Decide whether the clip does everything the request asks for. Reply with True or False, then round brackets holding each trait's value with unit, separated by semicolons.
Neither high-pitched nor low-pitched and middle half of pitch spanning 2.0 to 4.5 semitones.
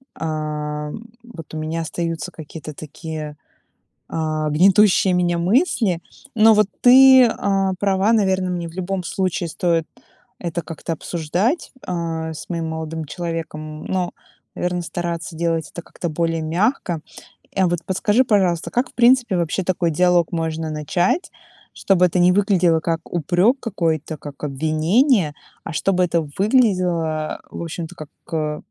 True (170 Hz; 3.1 semitones)